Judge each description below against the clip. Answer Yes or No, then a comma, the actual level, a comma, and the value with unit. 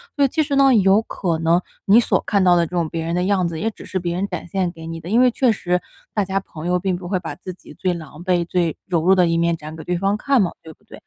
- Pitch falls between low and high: Yes, medium, 180 Hz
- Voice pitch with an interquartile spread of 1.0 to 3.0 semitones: Yes, average, 2.7 semitones